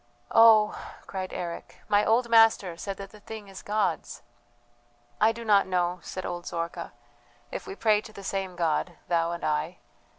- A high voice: Yes, high, 195 Hz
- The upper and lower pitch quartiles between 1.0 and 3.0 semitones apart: No, average, 3.7 semitones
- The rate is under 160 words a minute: No, average, 170 wpm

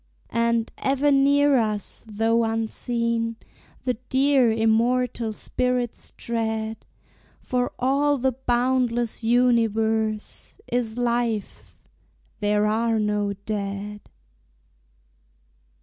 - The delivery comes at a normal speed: No, slow, 85 wpm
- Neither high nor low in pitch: No, high, 230 Hz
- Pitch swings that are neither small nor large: No, narrow, 2.2 semitones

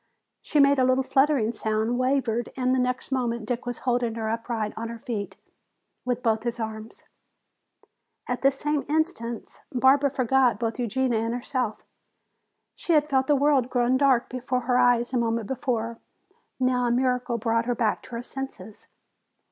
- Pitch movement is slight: Yes, narrow, 2.3 semitones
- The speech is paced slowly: No, average, 170 wpm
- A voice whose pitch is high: Yes, high, 245 Hz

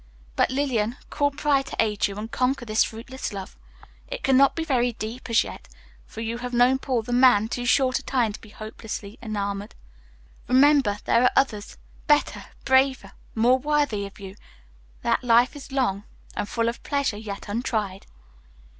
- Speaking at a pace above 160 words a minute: Yes, average, 170 wpm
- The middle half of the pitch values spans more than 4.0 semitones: No, average, 3.7 semitones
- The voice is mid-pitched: No, high, 240 Hz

